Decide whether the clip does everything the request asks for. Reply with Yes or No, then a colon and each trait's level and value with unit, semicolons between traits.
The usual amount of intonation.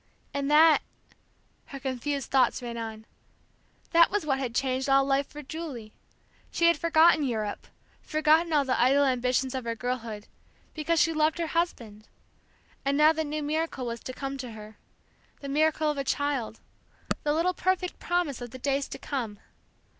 Yes: average, 3.8 semitones